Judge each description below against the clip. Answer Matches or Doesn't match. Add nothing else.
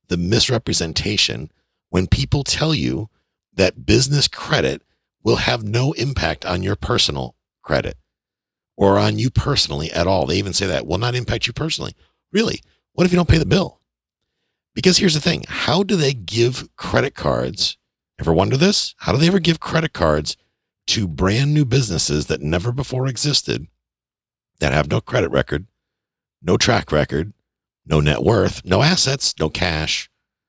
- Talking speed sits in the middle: Matches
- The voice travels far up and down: Matches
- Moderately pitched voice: Doesn't match